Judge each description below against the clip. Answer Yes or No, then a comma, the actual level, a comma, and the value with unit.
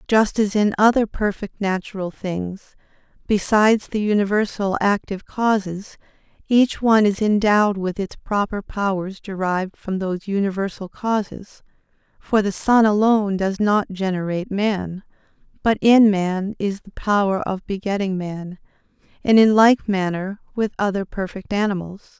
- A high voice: Yes, high, 200 Hz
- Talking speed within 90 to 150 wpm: Yes, slow, 135 wpm